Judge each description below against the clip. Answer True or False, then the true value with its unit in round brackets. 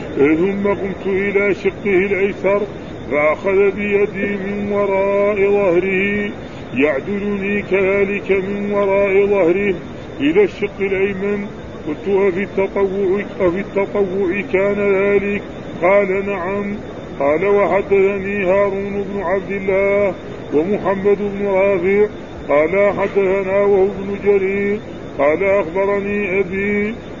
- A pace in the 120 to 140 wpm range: False (95 wpm)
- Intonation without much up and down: True (0.8 semitones)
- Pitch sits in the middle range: False (200 Hz)